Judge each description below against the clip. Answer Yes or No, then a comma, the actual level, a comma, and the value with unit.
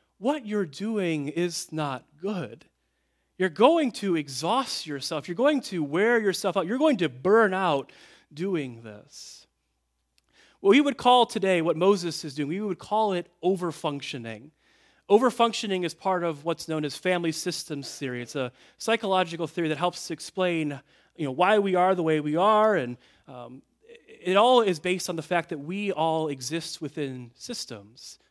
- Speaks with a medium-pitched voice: Yes, medium, 175 Hz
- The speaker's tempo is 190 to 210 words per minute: No, average, 165 wpm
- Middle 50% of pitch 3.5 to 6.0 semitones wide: Yes, average, 5.0 semitones